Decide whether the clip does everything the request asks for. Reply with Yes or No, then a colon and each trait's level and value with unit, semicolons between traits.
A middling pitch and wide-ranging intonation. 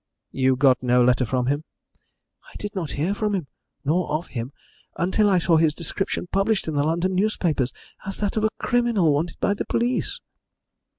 Yes: medium, 170 Hz; wide, 5.9 semitones